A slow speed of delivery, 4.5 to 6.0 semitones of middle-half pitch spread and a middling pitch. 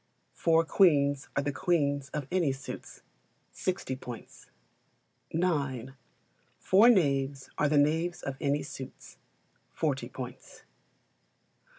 No: slow, 105 wpm; average, 3.6 semitones; medium, 145 Hz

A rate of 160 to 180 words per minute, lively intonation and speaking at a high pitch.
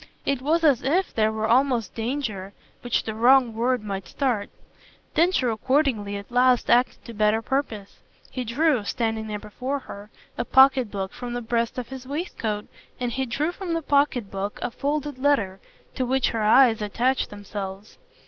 No: average, 175 wpm; average, 4.0 semitones; high, 240 Hz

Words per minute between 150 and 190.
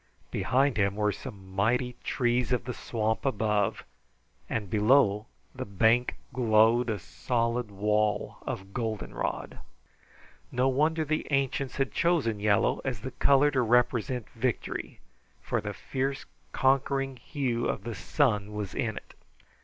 No: slow, 135 wpm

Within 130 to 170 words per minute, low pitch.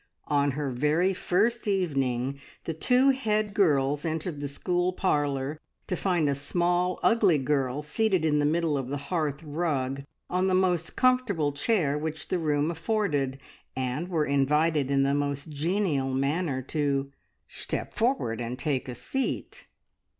No: average, 150 wpm; medium, 150 Hz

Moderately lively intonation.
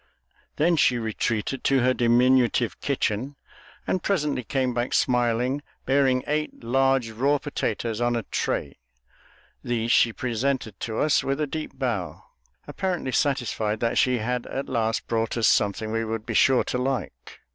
Yes: average, 3.0 semitones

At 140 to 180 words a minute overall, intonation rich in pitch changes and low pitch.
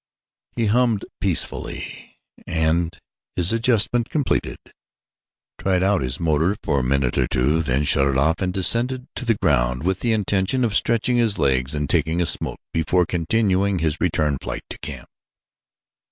Yes: average, 160 wpm; wide, 6.6 semitones; very low, 90 Hz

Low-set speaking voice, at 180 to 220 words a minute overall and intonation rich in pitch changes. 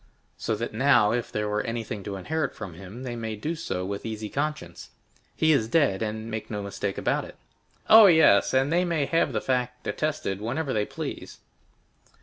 Yes: low, 115 Hz; average, 185 wpm; wide, 6.0 semitones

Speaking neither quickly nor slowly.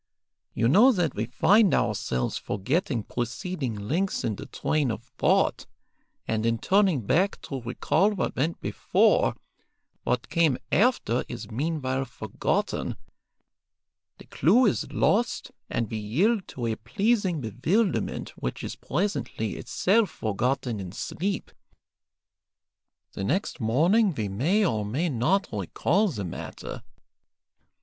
No: slow, 125 wpm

